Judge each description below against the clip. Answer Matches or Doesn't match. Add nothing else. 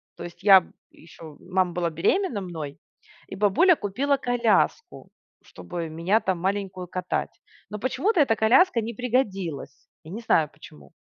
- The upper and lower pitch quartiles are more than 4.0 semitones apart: Matches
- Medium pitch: Doesn't match